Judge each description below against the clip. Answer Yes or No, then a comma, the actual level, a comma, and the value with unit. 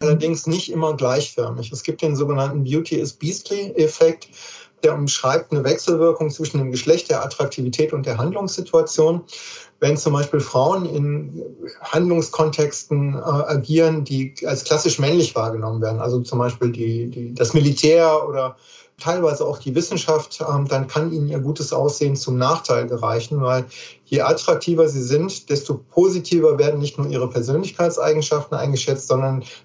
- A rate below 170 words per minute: Yes, average, 145 wpm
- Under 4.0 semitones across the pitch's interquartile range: Yes, average, 3.3 semitones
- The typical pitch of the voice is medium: Yes, medium, 150 Hz